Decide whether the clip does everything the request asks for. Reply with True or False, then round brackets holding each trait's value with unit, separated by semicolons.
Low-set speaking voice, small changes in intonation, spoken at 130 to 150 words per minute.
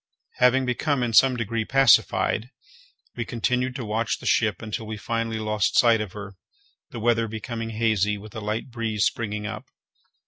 False (115 Hz; 1.9 semitones; 170 wpm)